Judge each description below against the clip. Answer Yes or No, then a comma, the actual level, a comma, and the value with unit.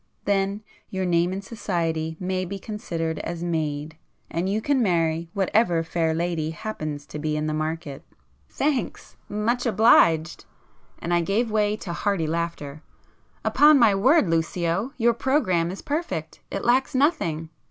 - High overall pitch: No, medium, 175 Hz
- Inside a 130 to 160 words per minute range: Yes, average, 140 wpm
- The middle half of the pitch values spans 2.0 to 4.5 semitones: No, average, 4.9 semitones